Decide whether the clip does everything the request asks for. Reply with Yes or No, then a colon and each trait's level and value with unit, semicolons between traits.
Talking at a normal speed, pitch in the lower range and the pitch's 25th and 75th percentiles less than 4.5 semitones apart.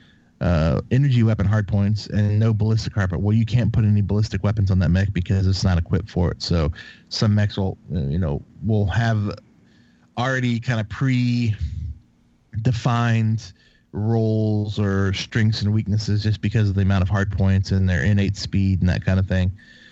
Yes: average, 180 wpm; low, 105 Hz; narrow, 2.4 semitones